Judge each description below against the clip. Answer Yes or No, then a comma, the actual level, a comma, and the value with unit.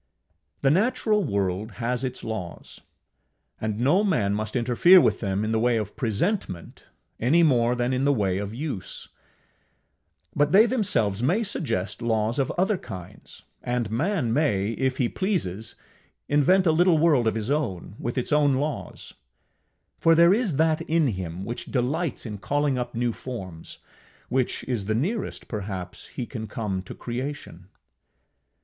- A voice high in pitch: No, low, 125 Hz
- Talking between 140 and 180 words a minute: Yes, average, 155 wpm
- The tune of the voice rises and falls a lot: Yes, wide, 6.3 semitones